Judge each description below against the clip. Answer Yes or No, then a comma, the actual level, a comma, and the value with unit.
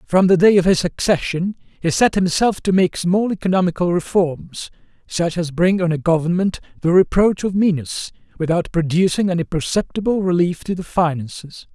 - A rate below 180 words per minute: Yes, average, 165 wpm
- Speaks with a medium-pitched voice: Yes, medium, 180 Hz